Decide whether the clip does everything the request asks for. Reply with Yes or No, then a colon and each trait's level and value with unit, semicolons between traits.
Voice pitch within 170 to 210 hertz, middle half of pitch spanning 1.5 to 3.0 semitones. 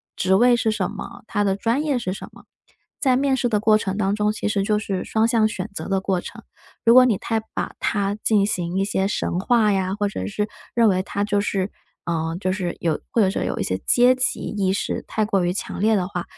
Yes: high, 205 Hz; narrow, 2.6 semitones